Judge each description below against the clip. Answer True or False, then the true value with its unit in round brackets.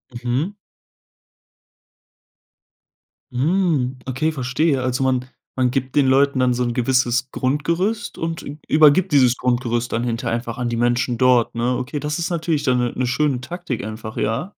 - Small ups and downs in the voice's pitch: False (3.5 semitones)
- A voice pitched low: True (130 Hz)